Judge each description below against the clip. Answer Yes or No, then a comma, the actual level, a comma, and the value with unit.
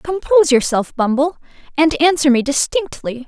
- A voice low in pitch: No, very high, 280 Hz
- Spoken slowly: Yes, slow, 130 wpm